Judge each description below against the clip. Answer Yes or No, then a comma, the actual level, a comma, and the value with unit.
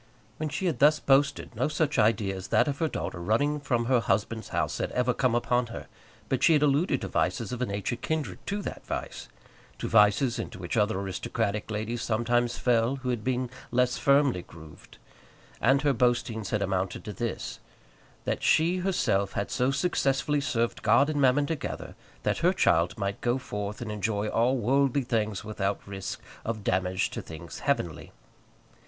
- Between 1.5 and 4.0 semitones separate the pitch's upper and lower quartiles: No, average, 4.8 semitones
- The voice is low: Yes, low, 120 Hz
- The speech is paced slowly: No, average, 180 wpm